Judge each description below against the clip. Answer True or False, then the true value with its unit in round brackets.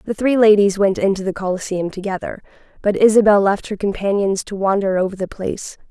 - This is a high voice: True (200 Hz)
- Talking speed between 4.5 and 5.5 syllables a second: False (5.9 syllables/s)